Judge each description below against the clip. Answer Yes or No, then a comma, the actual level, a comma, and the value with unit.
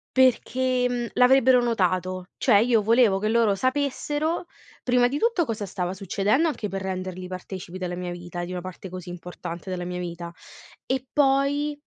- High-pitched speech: Yes, high, 205 Hz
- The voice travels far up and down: Yes, wide, 6.0 semitones